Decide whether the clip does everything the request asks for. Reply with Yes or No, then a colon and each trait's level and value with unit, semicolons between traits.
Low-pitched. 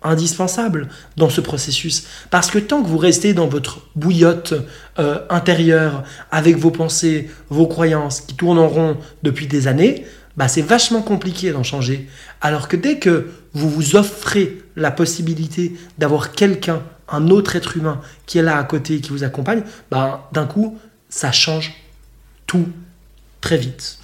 No: medium, 160 Hz